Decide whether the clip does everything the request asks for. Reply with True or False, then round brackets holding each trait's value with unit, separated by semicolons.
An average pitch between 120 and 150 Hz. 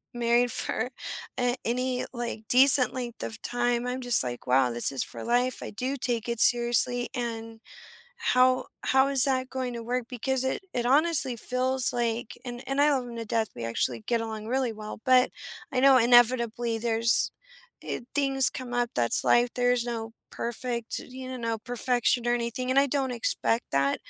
False (245 Hz)